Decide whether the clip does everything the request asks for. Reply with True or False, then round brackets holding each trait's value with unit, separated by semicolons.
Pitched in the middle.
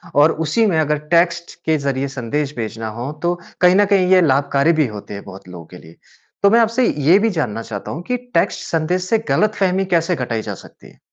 True (155 Hz)